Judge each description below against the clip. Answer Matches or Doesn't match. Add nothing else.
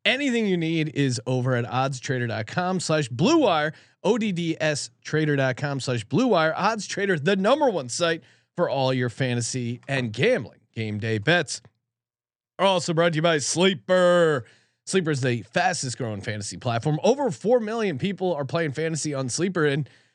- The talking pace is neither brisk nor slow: Matches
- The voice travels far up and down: Matches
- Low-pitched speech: Doesn't match